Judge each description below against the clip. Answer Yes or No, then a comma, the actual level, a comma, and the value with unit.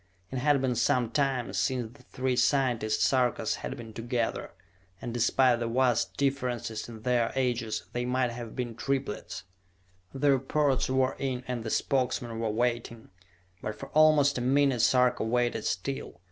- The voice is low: Yes, low, 125 Hz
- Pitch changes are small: Yes, narrow, 2.2 semitones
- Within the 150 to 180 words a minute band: Yes, average, 160 wpm